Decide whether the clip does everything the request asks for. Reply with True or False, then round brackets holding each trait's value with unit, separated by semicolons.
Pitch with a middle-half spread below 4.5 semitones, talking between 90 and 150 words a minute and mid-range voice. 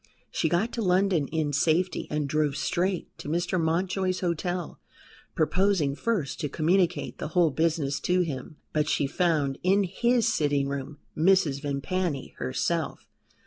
True (4.0 semitones; 145 wpm; 165 Hz)